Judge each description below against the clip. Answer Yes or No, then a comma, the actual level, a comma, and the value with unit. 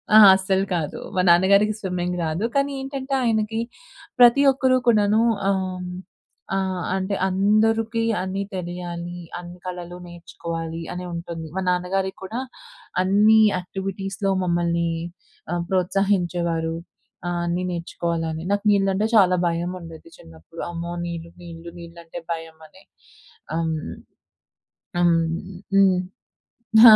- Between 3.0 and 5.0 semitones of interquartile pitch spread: No, narrow, 2.6 semitones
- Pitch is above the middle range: No, medium, 180 Hz